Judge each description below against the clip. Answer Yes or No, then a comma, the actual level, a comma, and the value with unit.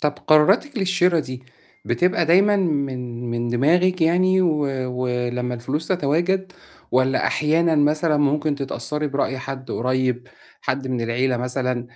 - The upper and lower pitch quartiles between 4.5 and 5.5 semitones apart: Yes, average, 5.1 semitones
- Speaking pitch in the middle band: Yes, medium, 145 Hz